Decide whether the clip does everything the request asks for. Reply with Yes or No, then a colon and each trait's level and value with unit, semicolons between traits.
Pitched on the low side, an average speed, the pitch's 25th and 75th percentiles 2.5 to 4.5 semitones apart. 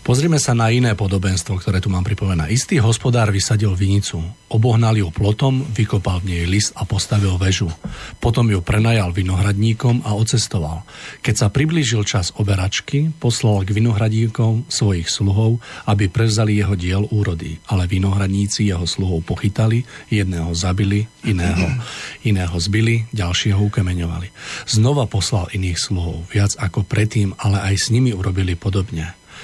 Yes: low, 105 Hz; average, 140 wpm; average, 2.9 semitones